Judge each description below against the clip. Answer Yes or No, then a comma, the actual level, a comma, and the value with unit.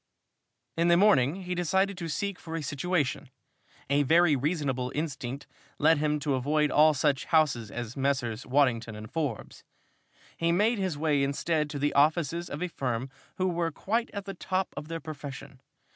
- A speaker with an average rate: Yes, average, 175 wpm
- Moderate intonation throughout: Yes, average, 4.0 semitones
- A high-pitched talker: No, medium, 150 Hz